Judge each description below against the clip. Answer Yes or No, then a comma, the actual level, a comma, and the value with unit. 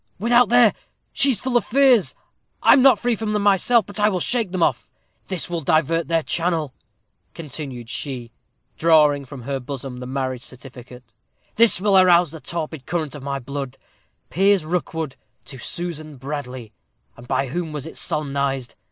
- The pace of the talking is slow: No, average, 170 wpm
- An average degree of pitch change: No, wide, 5.8 semitones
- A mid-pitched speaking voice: Yes, medium, 155 Hz